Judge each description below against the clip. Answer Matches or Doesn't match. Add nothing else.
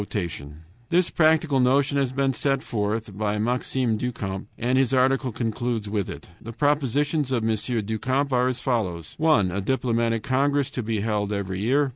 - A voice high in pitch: Doesn't match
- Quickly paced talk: Doesn't match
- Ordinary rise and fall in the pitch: Matches